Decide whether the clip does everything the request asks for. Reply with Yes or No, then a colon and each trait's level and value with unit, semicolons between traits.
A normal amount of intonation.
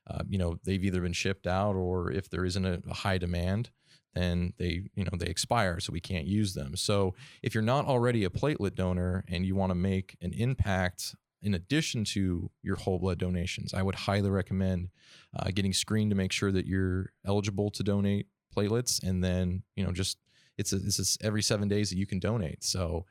No: narrow, 2.1 semitones